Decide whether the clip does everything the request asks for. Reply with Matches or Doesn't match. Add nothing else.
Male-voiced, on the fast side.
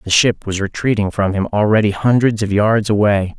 Doesn't match